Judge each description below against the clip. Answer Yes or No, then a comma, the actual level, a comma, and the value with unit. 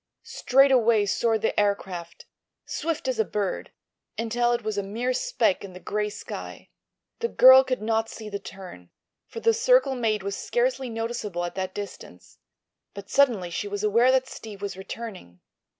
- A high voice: Yes, high, 220 Hz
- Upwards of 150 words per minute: Yes, average, 170 wpm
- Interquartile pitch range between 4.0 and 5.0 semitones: Yes, average, 4.3 semitones